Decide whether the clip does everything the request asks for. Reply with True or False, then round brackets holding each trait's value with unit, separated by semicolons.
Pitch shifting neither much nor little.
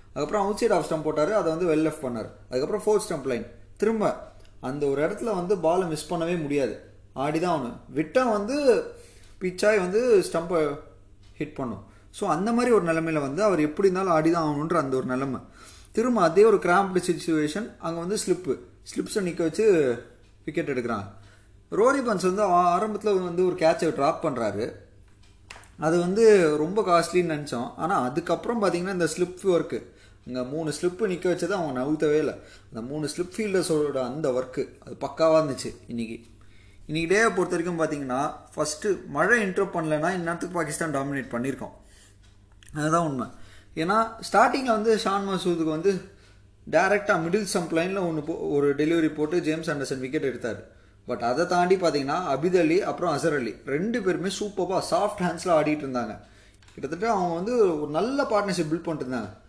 False (6.5 semitones)